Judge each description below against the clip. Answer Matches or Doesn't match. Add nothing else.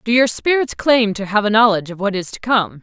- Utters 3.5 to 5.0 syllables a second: Doesn't match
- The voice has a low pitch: Doesn't match